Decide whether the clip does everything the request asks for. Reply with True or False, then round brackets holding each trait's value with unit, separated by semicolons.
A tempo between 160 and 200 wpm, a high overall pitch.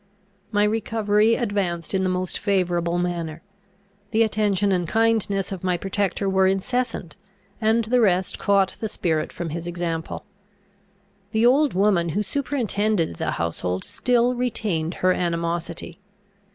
False (135 wpm; 195 Hz)